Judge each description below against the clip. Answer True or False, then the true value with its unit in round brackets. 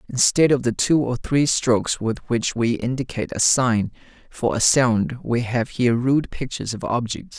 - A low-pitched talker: True (120 Hz)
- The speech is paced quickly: False (185 wpm)